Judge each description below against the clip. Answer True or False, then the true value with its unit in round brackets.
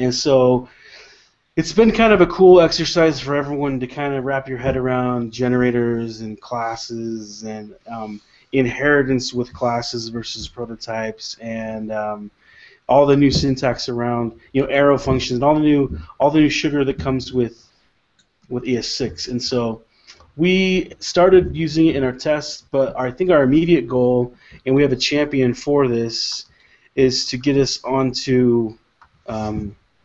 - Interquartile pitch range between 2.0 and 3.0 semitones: False (3.5 semitones)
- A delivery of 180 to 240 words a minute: False (160 wpm)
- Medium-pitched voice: False (125 Hz)